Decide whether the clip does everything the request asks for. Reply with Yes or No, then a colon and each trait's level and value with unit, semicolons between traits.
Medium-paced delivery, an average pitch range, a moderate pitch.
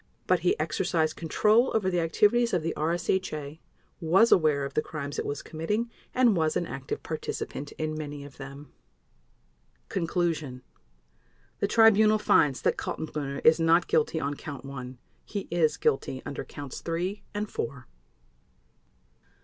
Yes: average, 145 wpm; average, 4.5 semitones; medium, 160 Hz